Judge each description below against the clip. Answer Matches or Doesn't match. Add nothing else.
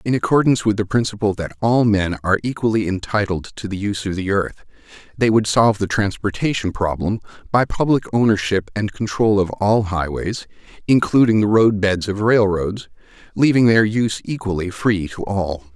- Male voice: Matches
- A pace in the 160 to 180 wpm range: Matches